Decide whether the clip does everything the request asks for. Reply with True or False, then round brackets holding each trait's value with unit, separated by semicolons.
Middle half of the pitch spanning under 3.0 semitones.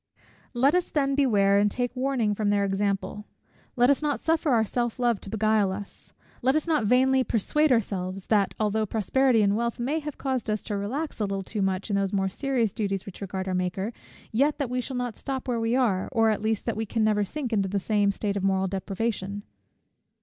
False (4.2 semitones)